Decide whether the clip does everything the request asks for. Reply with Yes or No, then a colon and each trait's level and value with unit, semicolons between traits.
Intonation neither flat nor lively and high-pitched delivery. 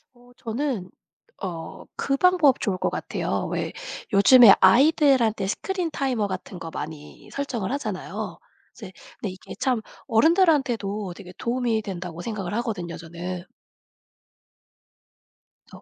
No: wide, 6.4 semitones; high, 220 Hz